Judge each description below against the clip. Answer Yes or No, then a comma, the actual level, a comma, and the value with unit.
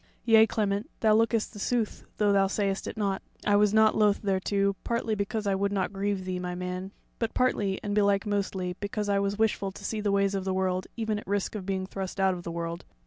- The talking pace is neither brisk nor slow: No, fast, 240 wpm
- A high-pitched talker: Yes, high, 200 Hz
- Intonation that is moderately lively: No, narrow, 1.7 semitones